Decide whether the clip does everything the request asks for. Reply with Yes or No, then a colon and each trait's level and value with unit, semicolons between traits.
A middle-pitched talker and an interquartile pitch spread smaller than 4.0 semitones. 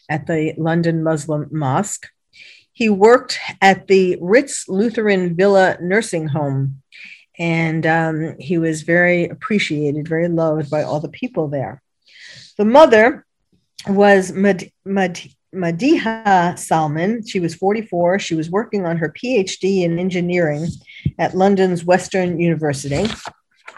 Yes: medium, 175 Hz; average, 3.5 semitones